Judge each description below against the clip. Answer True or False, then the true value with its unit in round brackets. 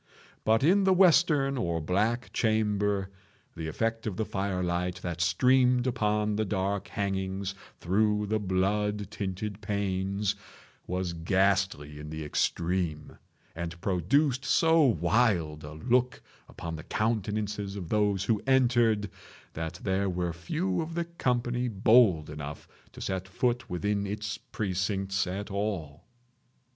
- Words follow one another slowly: True (130 wpm)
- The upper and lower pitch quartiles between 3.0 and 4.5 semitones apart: True (3.7 semitones)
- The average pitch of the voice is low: True (100 Hz)